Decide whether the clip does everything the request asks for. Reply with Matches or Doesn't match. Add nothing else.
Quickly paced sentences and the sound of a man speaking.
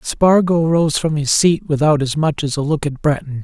Matches